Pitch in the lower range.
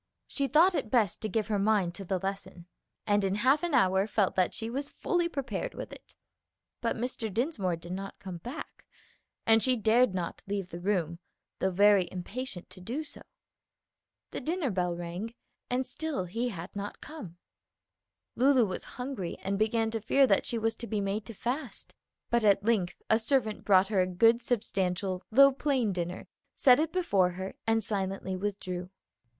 No: high, 210 Hz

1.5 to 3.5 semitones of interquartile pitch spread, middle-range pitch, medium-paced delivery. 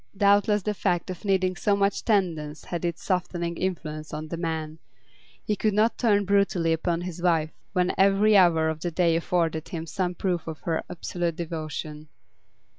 Yes: average, 3.2 semitones; medium, 175 Hz; average, 175 wpm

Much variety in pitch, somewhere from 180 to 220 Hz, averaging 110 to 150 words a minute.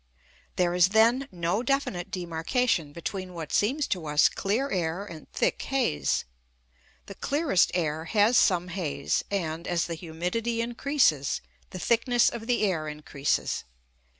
Yes: wide, 6.0 semitones; medium, 185 Hz; average, 140 wpm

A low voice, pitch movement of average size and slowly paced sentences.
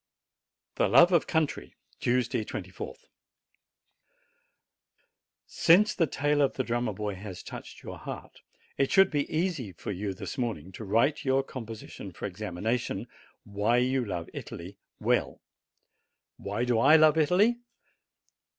No: low, 125 Hz; wide, 6.4 semitones; slow, 130 wpm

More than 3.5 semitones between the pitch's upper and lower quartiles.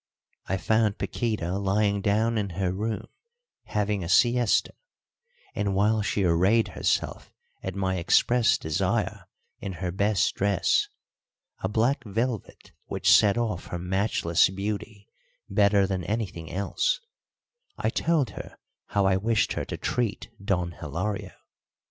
No: narrow, 2.6 semitones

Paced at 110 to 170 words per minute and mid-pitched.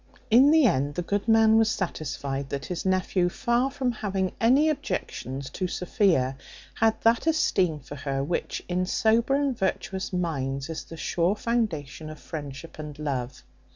Yes: average, 160 wpm; medium, 180 Hz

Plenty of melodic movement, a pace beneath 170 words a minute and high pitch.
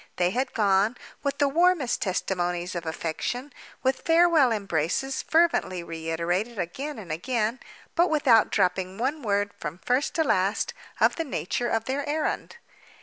Yes: wide, 7.5 semitones; average, 140 wpm; high, 225 Hz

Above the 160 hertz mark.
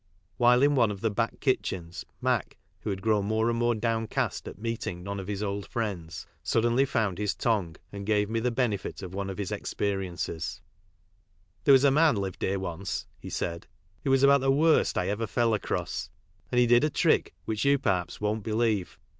No: low, 110 Hz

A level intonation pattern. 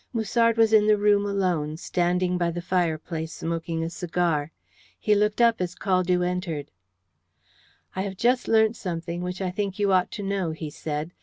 No: average, 3.5 semitones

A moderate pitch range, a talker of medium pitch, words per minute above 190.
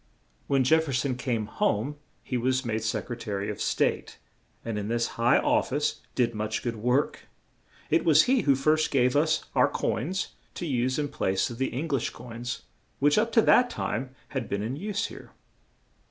No: average, 4.3 semitones; low, 130 Hz; average, 200 wpm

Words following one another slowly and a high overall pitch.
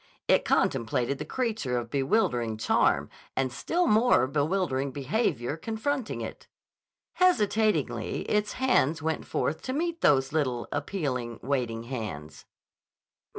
No: slow, 115 wpm; medium, 145 Hz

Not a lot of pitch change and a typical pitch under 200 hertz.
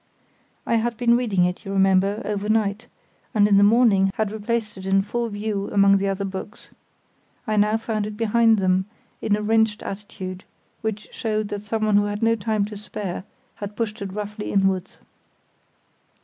No: narrow, 1.9 semitones; high, 210 Hz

